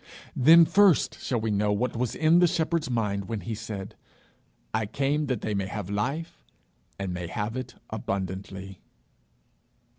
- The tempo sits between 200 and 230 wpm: No, average, 155 wpm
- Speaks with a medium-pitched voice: No, low, 110 Hz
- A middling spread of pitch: No, wide, 5.9 semitones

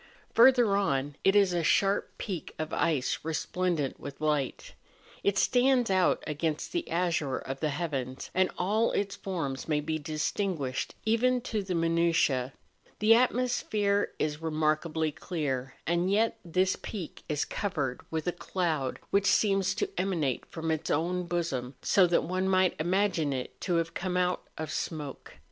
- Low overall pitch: No, medium, 170 Hz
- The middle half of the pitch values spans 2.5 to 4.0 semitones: No, average, 4.4 semitones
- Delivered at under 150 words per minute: No, average, 155 wpm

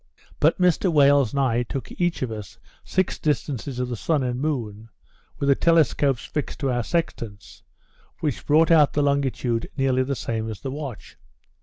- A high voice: No, low, 135 Hz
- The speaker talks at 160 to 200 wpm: Yes, average, 175 wpm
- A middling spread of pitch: Yes, average, 3.6 semitones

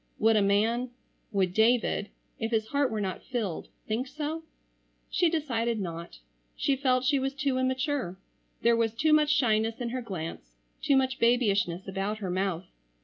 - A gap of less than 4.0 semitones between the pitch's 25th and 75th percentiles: No, average, 4.6 semitones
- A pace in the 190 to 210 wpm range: No, average, 150 wpm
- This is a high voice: Yes, high, 230 Hz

